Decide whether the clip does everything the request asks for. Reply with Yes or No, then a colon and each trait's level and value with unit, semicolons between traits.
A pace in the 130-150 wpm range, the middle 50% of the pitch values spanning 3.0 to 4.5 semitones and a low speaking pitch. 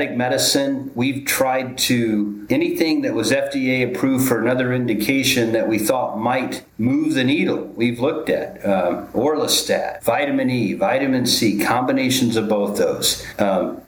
No: average, 145 wpm; narrow, 2.6 semitones; low, 130 Hz